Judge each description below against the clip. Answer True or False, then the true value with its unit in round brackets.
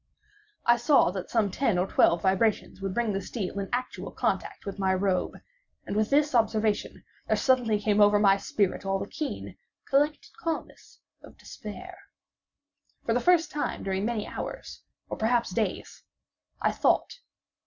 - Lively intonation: False (3.9 semitones)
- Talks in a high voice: True (215 Hz)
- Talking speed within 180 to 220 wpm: False (155 wpm)